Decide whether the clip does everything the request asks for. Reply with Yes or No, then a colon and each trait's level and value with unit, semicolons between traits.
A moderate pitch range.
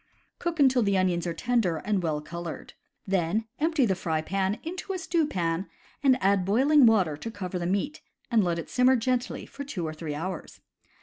No: wide, 6.9 semitones